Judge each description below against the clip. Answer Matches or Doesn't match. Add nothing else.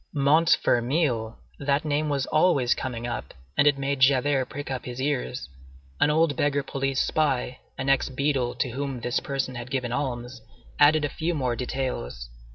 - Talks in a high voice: Doesn't match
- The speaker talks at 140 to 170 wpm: Matches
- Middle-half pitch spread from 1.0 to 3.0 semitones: Matches